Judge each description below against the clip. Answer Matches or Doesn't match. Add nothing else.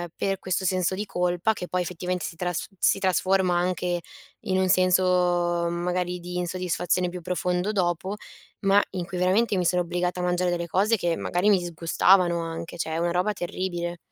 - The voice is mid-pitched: Matches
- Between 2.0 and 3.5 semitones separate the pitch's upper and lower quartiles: Doesn't match